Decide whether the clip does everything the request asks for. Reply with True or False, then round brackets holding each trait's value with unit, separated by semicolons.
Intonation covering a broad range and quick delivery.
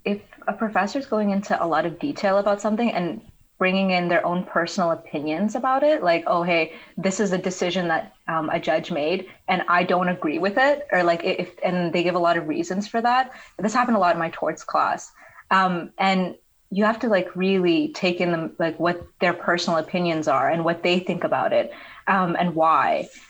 False (3.3 semitones; 215 wpm)